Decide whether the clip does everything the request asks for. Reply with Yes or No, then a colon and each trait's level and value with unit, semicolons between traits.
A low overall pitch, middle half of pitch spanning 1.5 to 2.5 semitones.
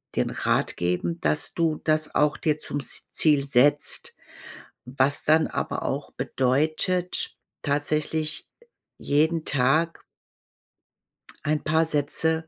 No: medium, 150 Hz; narrow, 2.0 semitones